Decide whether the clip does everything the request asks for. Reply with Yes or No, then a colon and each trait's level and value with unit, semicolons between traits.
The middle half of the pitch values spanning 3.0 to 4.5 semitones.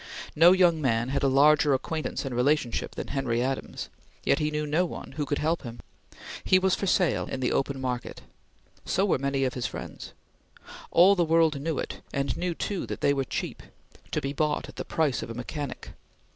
Yes: average, 3.5 semitones